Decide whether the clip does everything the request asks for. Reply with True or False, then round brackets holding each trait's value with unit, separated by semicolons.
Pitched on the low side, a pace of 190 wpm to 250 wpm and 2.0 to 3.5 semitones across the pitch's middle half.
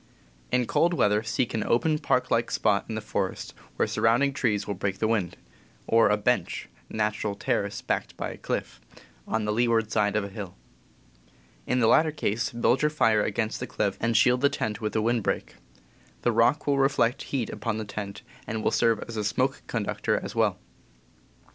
True (115 Hz; 195 wpm; 2.6 semitones)